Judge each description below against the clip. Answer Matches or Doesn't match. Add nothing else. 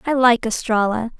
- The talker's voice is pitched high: Matches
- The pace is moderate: Matches